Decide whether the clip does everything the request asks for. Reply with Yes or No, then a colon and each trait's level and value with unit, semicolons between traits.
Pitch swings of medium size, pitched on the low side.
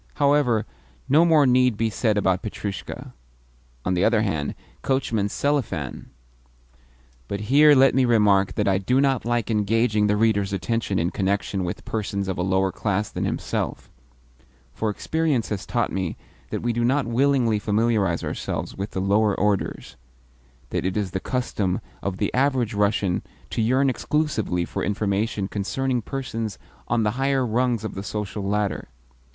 Yes: average, 4.2 semitones; low, 110 Hz